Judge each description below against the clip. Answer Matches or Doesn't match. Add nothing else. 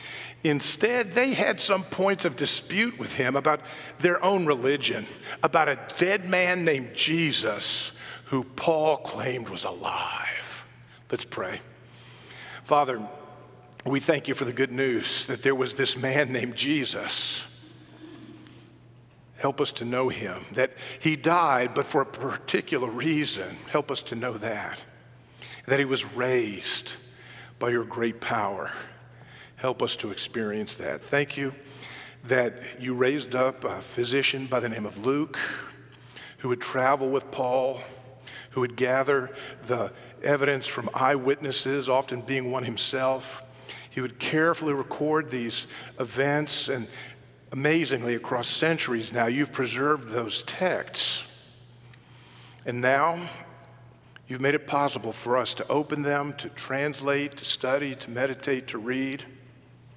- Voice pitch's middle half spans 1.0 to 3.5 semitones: Matches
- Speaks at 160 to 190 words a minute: Doesn't match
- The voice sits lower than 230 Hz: Matches